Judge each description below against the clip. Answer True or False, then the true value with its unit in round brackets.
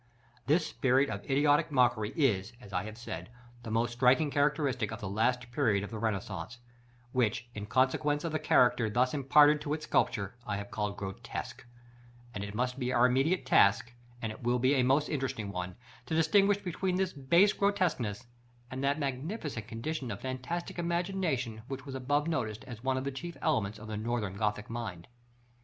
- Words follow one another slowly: False (185 wpm)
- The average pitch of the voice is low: True (125 Hz)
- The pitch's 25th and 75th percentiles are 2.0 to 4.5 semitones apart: False (5.2 semitones)